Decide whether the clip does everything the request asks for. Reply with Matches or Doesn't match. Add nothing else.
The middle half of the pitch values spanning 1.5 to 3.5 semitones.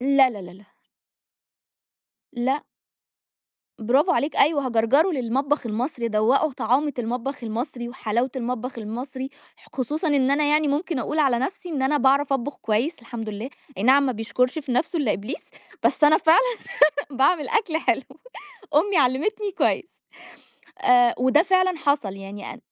Doesn't match